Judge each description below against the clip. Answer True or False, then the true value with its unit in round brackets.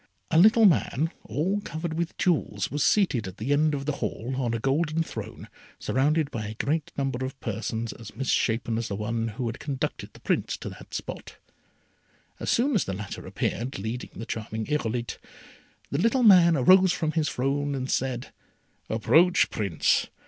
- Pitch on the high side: False (135 Hz)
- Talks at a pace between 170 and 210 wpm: True (180 wpm)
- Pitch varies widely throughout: True (5.9 semitones)